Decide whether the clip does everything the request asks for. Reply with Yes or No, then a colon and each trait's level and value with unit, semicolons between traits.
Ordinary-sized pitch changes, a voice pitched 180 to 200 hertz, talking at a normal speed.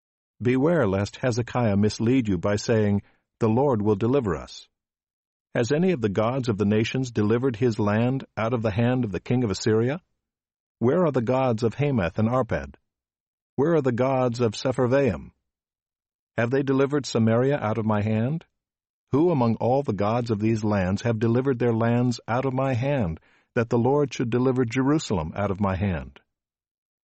No: average, 3.5 semitones; low, 120 Hz; average, 180 wpm